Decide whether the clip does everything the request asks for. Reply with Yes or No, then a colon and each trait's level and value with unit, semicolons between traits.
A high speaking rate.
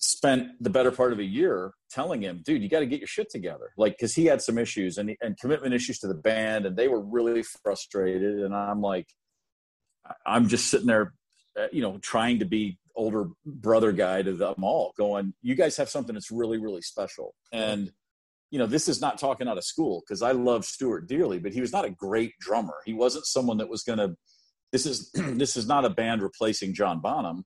Yes: fast, 220 wpm